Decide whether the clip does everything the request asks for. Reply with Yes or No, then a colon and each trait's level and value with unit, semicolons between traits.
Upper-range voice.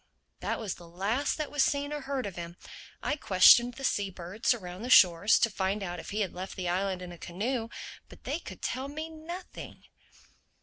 Yes: high, 205 Hz